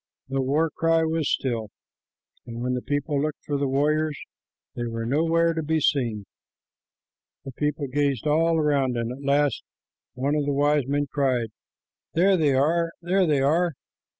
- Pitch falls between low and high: Yes, medium, 145 Hz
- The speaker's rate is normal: Yes, average, 165 wpm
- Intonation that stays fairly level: No, average, 3.0 semitones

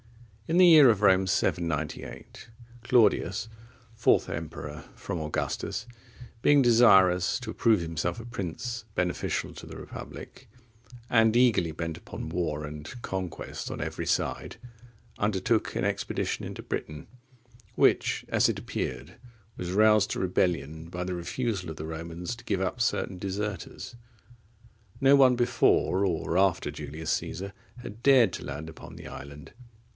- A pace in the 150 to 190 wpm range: No, average, 140 wpm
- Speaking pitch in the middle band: No, very low, 95 Hz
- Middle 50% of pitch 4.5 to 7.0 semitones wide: Yes, wide, 5.6 semitones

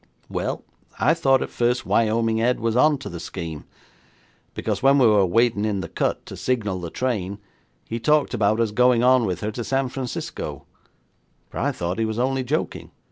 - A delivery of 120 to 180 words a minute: No, average, 190 wpm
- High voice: No, low, 115 Hz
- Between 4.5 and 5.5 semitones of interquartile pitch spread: No, average, 3.6 semitones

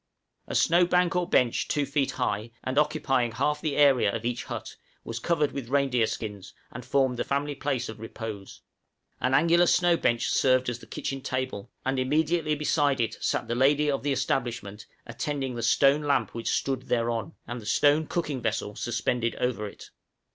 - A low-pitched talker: Yes, low, 130 Hz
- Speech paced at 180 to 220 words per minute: Yes, average, 185 wpm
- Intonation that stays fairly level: No, average, 3.8 semitones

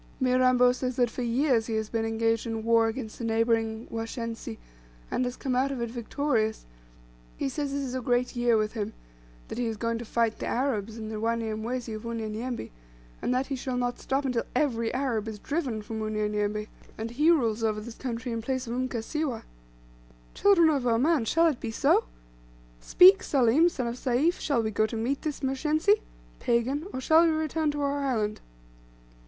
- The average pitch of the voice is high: Yes, high, 240 Hz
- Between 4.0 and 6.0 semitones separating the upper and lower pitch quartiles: No, average, 3.2 semitones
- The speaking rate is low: No, average, 195 wpm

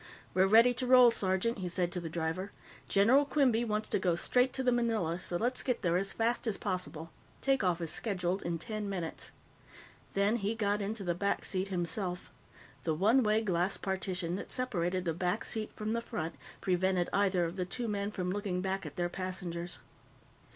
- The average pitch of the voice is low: No, high, 190 Hz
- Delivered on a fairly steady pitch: No, average, 3.8 semitones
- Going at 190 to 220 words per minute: Yes, average, 195 wpm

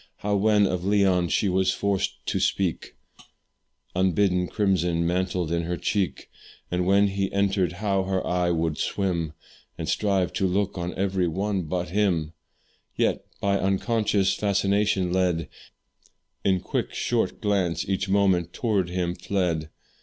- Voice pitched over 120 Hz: No, very low, 95 Hz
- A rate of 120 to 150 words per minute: Yes, average, 140 wpm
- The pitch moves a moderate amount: No, narrow, 2.1 semitones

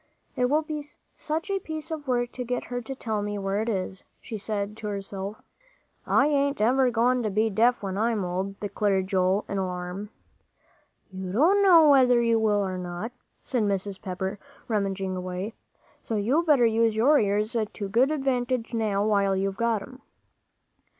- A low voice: No, high, 215 Hz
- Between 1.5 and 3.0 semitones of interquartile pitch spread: No, average, 4.2 semitones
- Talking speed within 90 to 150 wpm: No, average, 175 wpm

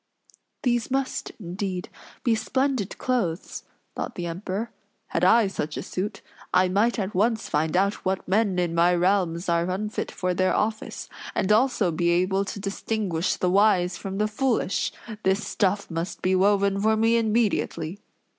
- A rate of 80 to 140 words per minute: No, average, 160 wpm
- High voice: Yes, high, 195 Hz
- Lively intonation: No, average, 3.3 semitones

